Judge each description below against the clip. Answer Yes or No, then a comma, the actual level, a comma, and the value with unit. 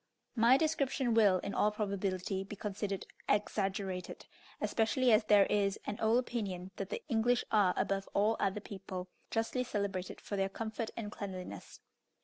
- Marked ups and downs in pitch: No, narrow, 2.6 semitones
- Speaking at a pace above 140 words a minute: Yes, average, 150 wpm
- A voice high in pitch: Yes, high, 205 Hz